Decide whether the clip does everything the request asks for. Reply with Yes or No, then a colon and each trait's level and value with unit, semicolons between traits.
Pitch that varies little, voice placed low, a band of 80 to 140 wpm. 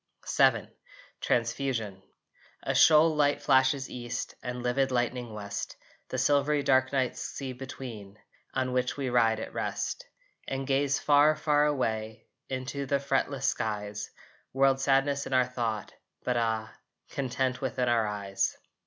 No: average, 3.0 semitones; low, 130 Hz; slow, 135 wpm